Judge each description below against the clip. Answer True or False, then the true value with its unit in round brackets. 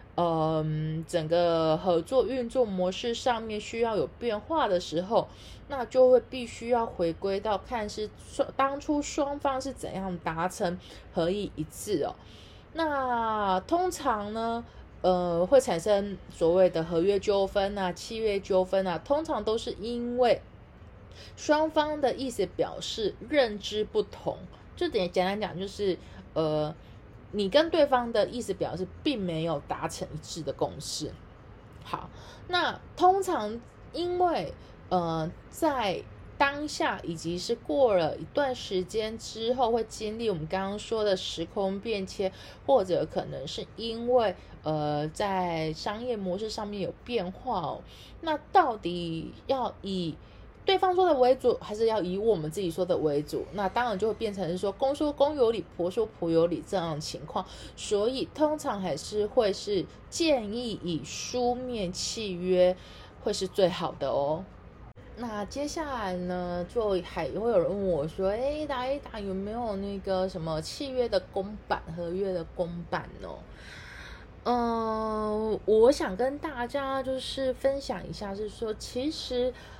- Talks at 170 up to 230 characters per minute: True (215 characters per minute)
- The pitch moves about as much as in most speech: False (5.9 semitones)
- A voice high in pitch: True (210 Hz)